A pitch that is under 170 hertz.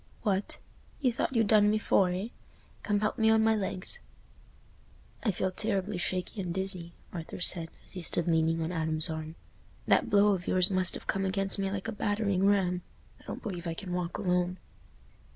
No: high, 190 Hz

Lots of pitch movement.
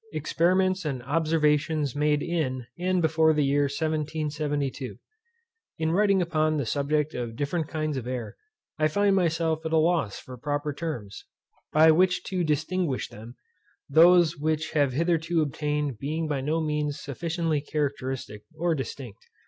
No: narrow, 2.5 semitones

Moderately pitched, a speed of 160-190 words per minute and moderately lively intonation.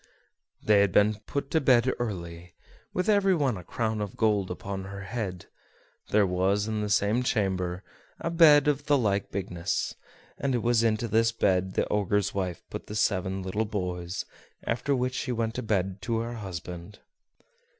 No: low, 105 Hz; average, 175 wpm; average, 4.0 semitones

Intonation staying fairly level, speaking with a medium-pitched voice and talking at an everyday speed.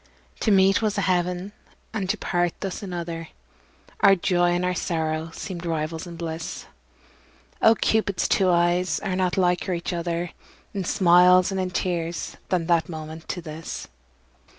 Yes: narrow, 1.9 semitones; medium, 175 Hz; average, 155 wpm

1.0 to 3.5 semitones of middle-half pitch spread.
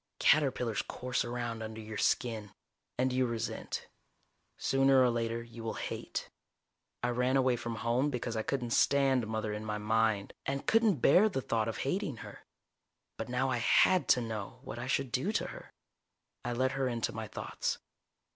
Yes: average, 2.9 semitones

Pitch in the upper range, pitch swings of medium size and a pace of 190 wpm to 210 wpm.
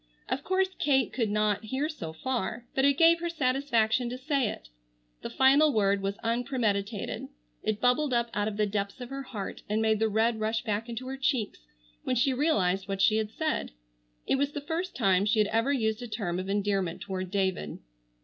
Yes: high, 225 Hz; average, 4.7 semitones; fast, 205 wpm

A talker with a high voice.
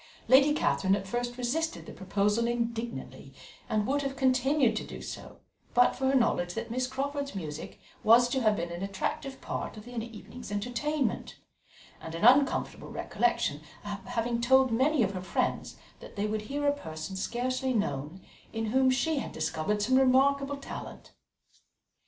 Yes: high, 240 Hz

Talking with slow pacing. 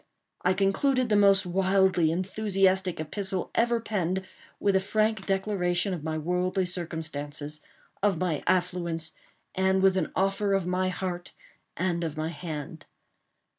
Yes: slow, 130 wpm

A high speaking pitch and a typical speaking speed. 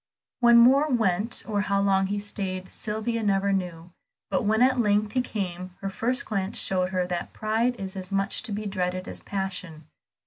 Yes: high, 200 Hz; average, 185 wpm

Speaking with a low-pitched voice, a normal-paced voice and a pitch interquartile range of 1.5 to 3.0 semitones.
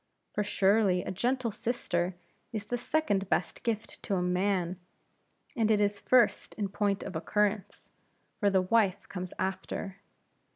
No: high, 200 Hz; average, 150 wpm; narrow, 2.6 semitones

